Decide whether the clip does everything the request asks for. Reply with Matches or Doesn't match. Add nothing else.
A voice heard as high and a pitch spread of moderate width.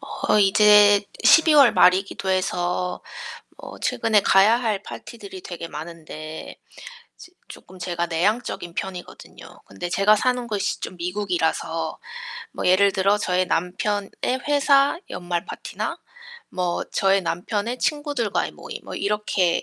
Matches